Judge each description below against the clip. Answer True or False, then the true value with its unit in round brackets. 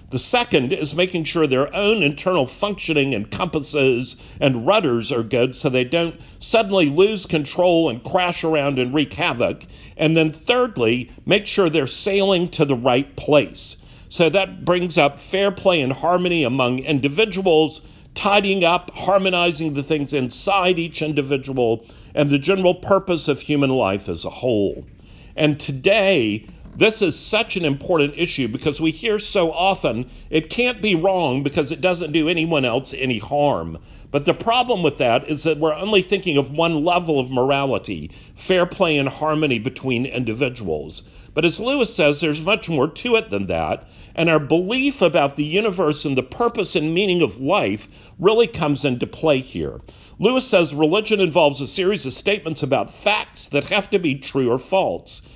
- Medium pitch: True (155 Hz)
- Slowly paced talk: False (170 wpm)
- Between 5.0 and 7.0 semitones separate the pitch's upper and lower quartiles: True (5.4 semitones)